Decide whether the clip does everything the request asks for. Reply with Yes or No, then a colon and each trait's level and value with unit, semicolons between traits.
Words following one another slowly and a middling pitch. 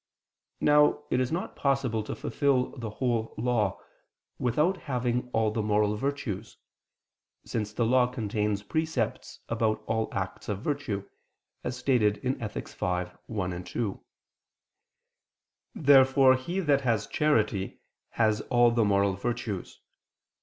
No: slow, 125 wpm; low, 115 Hz